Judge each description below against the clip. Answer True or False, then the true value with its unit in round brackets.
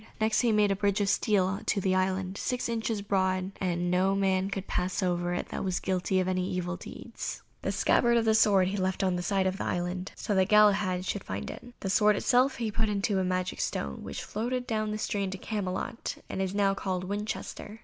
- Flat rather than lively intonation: True (2.3 semitones)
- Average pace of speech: False (225 wpm)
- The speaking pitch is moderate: False (195 Hz)